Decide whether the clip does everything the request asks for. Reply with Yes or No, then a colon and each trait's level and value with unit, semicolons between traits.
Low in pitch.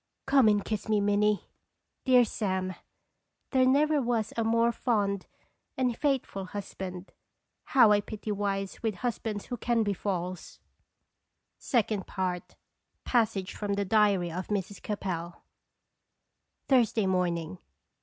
No: high, 210 Hz